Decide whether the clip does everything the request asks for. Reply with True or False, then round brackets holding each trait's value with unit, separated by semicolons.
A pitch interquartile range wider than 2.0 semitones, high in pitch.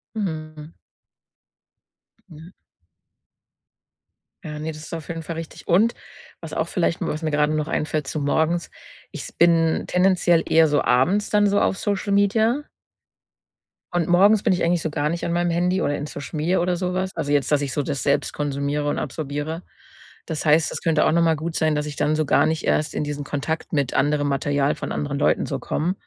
False (2.9 semitones; 160 Hz)